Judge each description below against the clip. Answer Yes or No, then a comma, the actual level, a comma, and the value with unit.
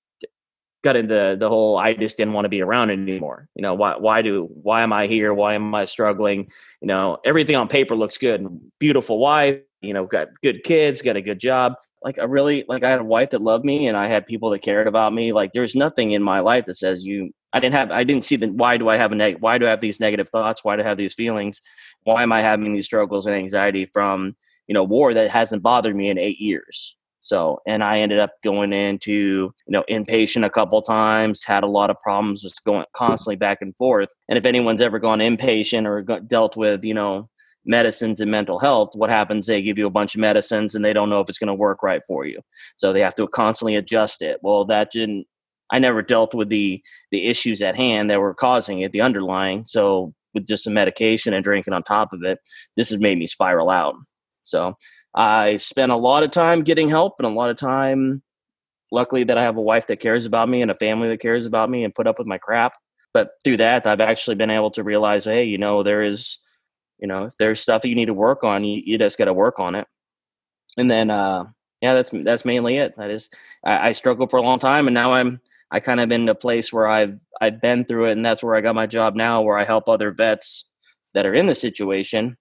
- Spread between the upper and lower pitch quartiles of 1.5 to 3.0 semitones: Yes, narrow, 2.4 semitones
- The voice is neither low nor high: No, low, 110 Hz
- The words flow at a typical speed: No, fast, 245 wpm